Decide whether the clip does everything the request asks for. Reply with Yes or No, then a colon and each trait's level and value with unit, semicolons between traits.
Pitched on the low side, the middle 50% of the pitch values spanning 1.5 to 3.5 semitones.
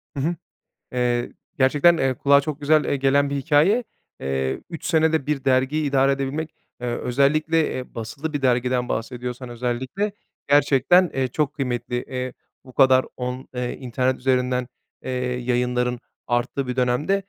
Yes: low, 130 Hz; average, 2.9 semitones